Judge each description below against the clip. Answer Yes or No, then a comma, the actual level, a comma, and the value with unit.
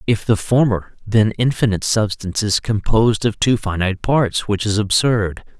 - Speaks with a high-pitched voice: No, low, 105 Hz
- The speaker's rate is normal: Yes, average, 160 wpm